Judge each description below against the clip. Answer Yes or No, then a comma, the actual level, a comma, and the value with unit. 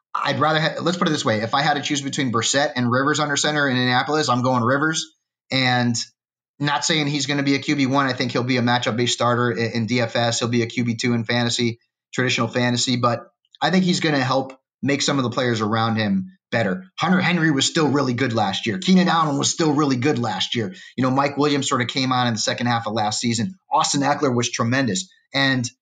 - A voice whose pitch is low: Yes, low, 130 Hz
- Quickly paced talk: Yes, fast, 245 wpm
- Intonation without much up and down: No, average, 3.4 semitones